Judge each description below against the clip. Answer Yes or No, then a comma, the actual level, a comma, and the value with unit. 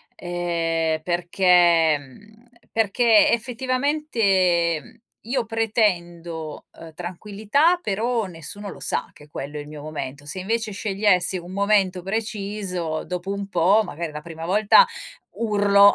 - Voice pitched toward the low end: No, high, 190 Hz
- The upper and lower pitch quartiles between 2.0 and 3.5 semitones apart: No, average, 4.2 semitones